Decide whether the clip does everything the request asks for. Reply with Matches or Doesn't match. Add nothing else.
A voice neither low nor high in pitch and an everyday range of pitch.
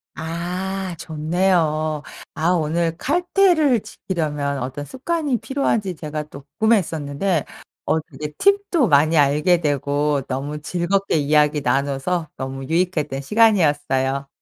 Matches